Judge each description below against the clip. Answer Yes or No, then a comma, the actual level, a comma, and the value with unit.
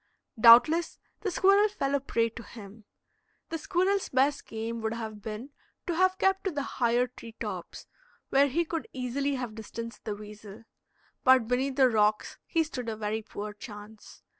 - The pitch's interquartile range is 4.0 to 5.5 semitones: Yes, average, 4.8 semitones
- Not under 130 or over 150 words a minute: No, average, 170 wpm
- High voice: Yes, high, 245 Hz